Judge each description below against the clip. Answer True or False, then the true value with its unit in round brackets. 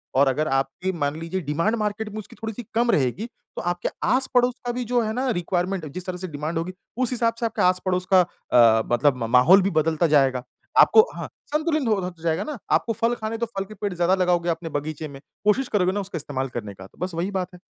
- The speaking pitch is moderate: True (180 Hz)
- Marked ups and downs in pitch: True (5.8 semitones)